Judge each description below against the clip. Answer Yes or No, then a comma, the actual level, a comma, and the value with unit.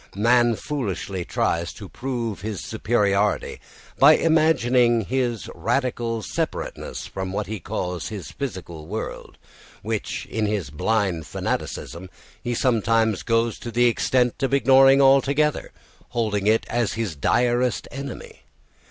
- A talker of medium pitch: No, low, 115 Hz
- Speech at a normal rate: No, slow, 125 wpm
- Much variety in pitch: No, average, 3.8 semitones